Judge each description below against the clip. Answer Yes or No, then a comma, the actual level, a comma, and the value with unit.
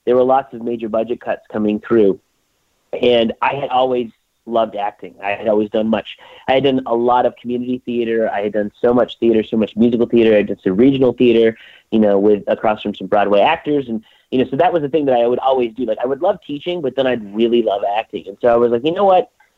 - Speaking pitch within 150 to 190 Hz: No, low, 120 Hz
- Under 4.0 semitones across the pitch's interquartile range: Yes, average, 2.8 semitones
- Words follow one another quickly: Yes, fast, 255 wpm